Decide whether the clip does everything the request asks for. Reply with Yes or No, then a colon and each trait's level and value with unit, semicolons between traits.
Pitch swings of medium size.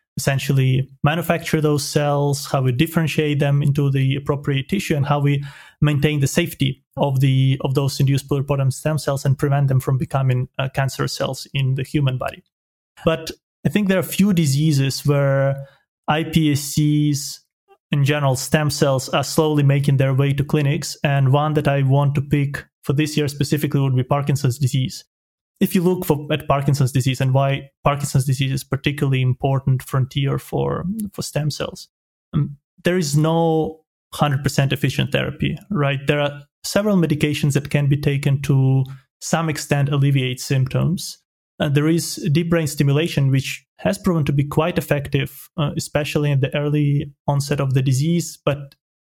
No: narrow, 2.0 semitones